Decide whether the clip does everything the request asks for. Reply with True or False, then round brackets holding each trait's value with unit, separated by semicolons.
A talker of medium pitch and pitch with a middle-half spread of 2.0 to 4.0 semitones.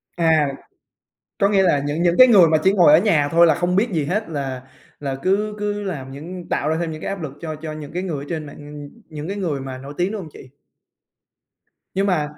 False (160 Hz; 4.4 semitones)